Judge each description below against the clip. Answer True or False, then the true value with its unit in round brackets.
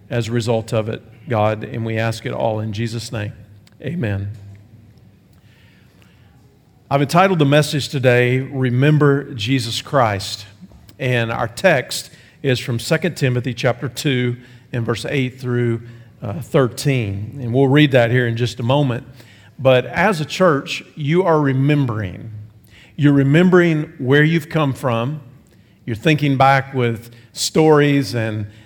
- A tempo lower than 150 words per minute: True (140 wpm)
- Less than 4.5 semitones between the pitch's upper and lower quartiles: True (3.9 semitones)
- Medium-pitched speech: False (125 Hz)